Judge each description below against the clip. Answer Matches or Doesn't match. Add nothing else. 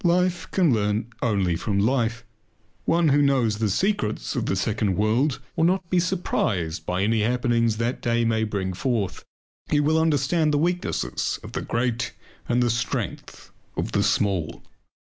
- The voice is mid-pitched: Doesn't match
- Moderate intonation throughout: Doesn't match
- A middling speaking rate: Matches